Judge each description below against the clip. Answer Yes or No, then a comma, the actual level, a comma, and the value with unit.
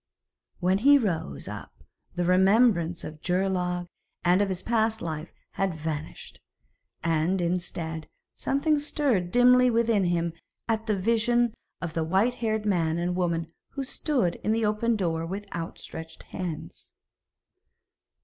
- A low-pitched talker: No, medium, 185 Hz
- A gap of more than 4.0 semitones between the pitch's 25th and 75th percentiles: Yes, average, 5.0 semitones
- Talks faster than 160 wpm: No, slow, 135 wpm